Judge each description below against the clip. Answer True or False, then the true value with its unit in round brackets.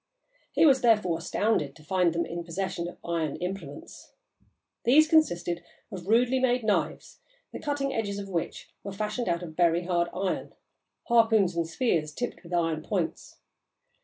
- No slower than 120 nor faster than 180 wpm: True (160 wpm)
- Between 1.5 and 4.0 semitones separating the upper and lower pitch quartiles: False (4.9 semitones)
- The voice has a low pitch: False (185 Hz)